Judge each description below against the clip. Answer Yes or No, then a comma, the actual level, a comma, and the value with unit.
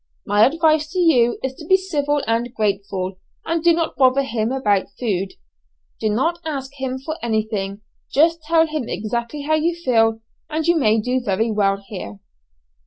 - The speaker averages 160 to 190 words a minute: Yes, average, 175 wpm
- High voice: Yes, very high, 255 Hz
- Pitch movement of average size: No, wide, 6.5 semitones